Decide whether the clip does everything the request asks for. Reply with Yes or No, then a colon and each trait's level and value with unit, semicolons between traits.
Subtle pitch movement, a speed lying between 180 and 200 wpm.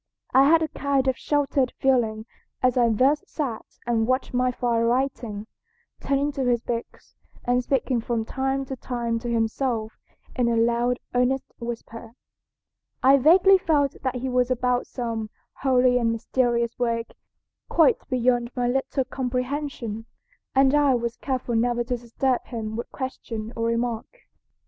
No: narrow, 2.3 semitones; average, 150 wpm